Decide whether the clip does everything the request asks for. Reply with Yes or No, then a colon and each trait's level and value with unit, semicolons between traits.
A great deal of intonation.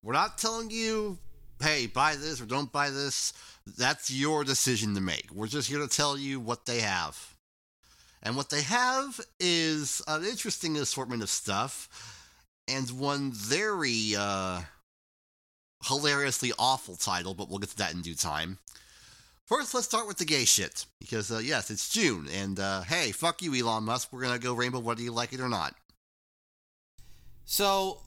Yes: wide, 6.7 semitones